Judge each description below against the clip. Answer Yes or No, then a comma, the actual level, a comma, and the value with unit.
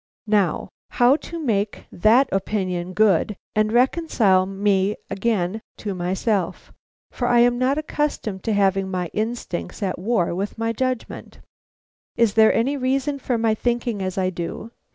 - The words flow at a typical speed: Yes, average, 150 wpm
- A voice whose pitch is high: Yes, high, 215 Hz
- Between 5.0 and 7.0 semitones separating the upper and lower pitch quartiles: No, average, 4.1 semitones